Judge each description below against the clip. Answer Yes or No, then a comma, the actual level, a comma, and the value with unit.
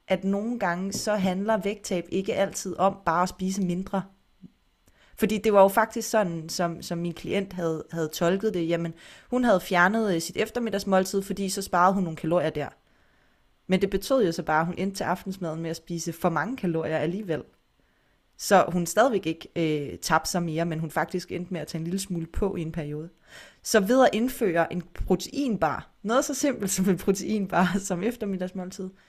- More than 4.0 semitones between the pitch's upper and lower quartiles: No, average, 3.1 semitones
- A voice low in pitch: No, medium, 185 Hz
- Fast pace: No, average, 195 wpm